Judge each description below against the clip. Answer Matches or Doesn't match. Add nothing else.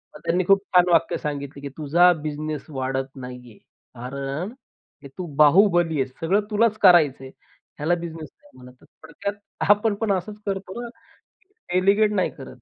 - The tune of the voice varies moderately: Doesn't match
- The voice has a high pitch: Doesn't match